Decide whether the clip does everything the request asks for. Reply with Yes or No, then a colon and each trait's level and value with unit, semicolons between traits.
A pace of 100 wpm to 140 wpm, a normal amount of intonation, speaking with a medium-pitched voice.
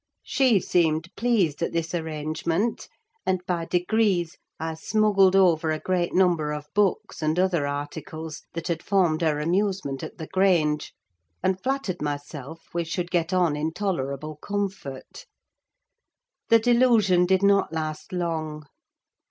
Yes: slow, 135 wpm; average, 3.5 semitones; medium, 175 Hz